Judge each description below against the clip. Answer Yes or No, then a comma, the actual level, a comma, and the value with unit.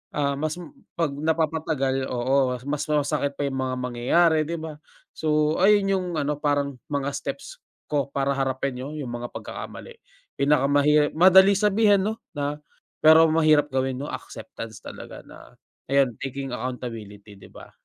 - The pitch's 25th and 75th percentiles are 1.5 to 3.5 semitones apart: Yes, average, 3.1 semitones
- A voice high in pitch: No, medium, 145 Hz